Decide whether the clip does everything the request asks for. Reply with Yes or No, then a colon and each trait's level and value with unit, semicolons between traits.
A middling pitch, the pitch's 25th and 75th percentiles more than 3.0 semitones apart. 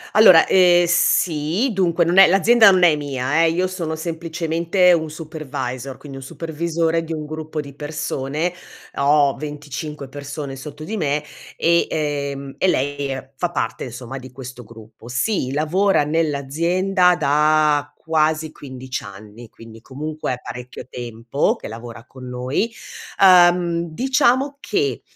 Yes: medium, 155 Hz; average, 4.1 semitones